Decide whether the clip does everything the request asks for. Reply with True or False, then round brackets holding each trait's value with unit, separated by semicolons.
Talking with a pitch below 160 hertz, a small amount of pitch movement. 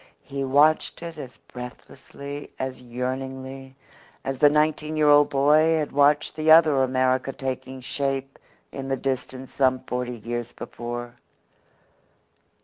True (135 Hz; 2.2 semitones)